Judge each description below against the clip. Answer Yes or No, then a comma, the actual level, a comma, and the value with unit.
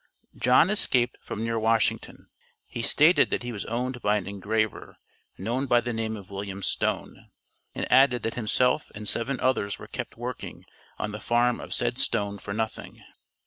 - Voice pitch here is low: Yes, low, 115 Hz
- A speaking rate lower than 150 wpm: No, average, 175 wpm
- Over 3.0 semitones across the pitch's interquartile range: No, average, 2.7 semitones